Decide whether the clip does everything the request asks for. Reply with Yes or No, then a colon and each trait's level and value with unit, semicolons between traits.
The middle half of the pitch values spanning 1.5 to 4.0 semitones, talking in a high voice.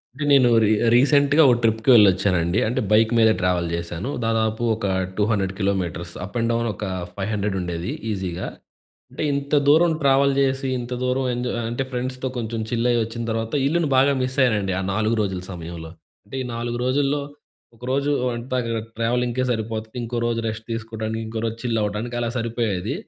No: average, 3.6 semitones; low, 115 Hz